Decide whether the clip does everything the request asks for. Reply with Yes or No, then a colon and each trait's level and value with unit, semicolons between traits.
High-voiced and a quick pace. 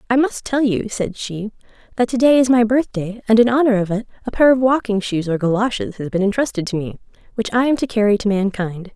Yes: high, 220 Hz; fast, 240 wpm